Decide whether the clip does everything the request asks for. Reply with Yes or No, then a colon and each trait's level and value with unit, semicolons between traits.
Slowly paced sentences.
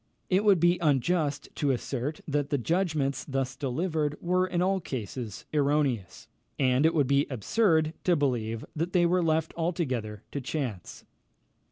No: average, 155 wpm